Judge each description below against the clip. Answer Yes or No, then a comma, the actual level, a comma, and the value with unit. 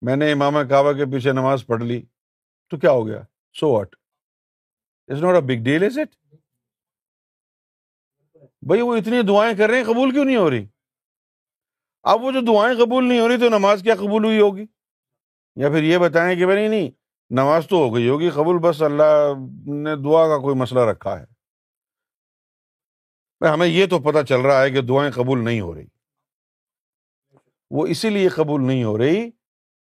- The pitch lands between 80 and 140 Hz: No, medium, 150 Hz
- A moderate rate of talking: Yes, average, 165 wpm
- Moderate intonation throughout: No, wide, 7.5 semitones